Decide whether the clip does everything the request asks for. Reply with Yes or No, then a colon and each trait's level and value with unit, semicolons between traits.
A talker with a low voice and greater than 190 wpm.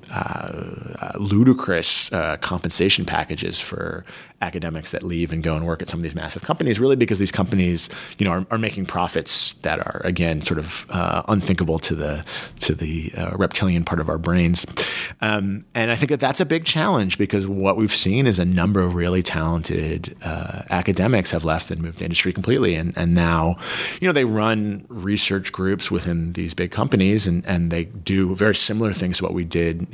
Yes: very low, 95 Hz; average, 200 wpm